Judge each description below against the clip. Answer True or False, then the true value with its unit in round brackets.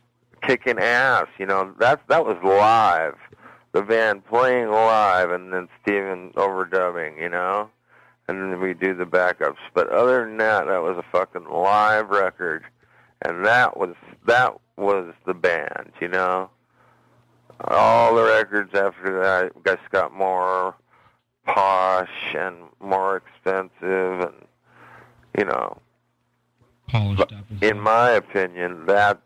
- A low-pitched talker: True (95 Hz)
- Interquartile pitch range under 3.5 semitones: True (2.9 semitones)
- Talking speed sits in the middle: False (130 wpm)